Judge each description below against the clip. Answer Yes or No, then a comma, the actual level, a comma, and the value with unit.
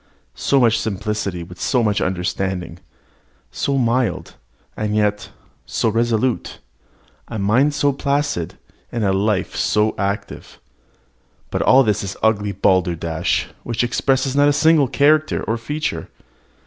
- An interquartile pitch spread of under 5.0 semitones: No, average, 5.3 semitones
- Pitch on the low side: Yes, low, 110 Hz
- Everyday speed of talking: No, slow, 130 wpm